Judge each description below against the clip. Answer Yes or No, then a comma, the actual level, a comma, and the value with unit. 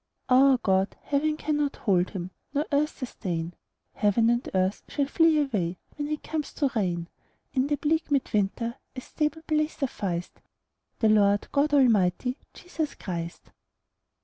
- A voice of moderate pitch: No, very high, 255 Hz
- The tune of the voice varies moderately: No, wide, 7.3 semitones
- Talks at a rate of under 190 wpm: Yes, average, 150 wpm